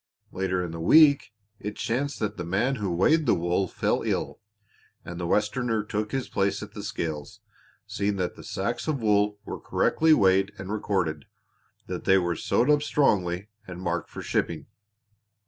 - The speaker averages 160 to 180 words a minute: Yes, average, 175 wpm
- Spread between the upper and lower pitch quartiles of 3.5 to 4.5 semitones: Yes, average, 4.1 semitones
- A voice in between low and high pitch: No, low, 100 Hz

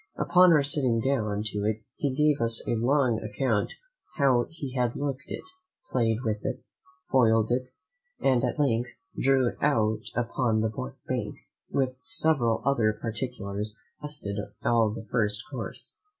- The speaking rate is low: No, average, 150 wpm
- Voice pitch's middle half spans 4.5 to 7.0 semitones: No, average, 3.7 semitones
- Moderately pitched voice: No, low, 120 Hz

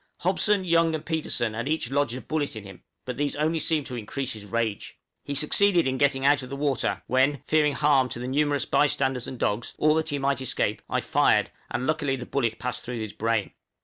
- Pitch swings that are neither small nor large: Yes, average, 3.5 semitones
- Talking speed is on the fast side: Yes, fast, 225 wpm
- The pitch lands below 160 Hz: Yes, medium, 140 Hz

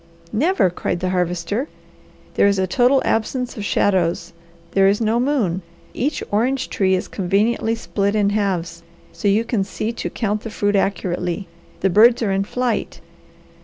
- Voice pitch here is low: No, high, 205 Hz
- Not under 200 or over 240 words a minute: No, average, 165 wpm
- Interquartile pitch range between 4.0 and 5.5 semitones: No, average, 3.6 semitones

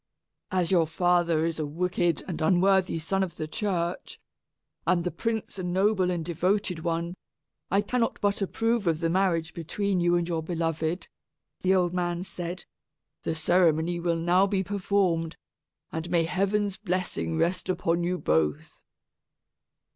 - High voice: No, medium, 175 Hz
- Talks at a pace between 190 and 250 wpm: No, average, 150 wpm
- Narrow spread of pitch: Yes, narrow, 2.3 semitones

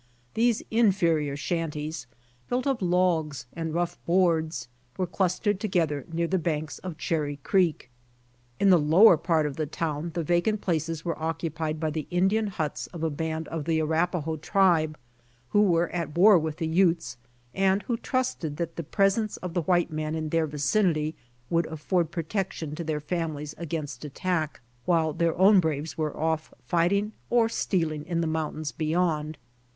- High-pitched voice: No, medium, 165 Hz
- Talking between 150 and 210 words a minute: Yes, average, 170 wpm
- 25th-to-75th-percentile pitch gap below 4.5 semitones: Yes, average, 2.8 semitones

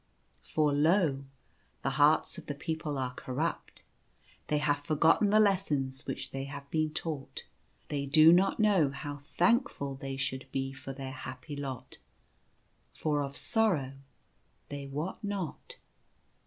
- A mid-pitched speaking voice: Yes, medium, 145 Hz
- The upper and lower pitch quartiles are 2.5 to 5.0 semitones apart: Yes, average, 3.0 semitones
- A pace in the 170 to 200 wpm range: No, average, 140 wpm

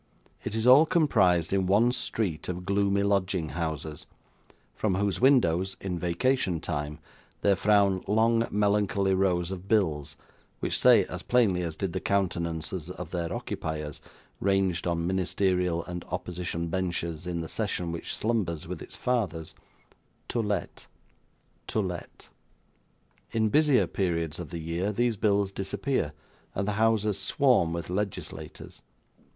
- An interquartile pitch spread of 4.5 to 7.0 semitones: No, average, 3.6 semitones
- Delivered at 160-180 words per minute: No, average, 140 wpm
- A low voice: Yes, very low, 95 Hz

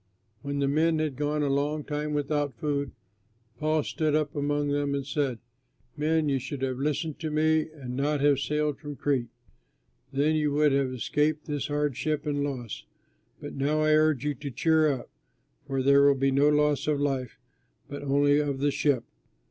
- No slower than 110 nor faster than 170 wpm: No, average, 185 wpm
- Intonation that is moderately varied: No, narrow, 1.5 semitones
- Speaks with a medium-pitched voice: Yes, medium, 145 Hz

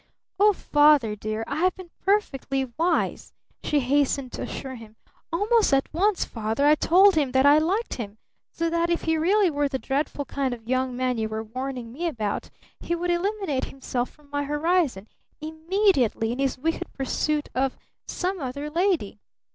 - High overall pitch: Yes, very high, 290 Hz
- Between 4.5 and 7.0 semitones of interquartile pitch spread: Yes, average, 5.1 semitones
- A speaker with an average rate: Yes, average, 175 wpm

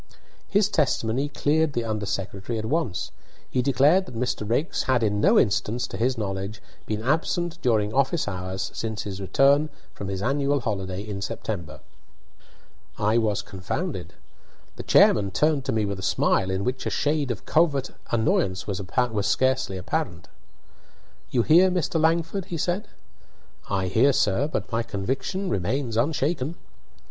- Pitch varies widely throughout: Yes, wide, 6.5 semitones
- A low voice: Yes, low, 120 Hz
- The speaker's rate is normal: Yes, average, 155 wpm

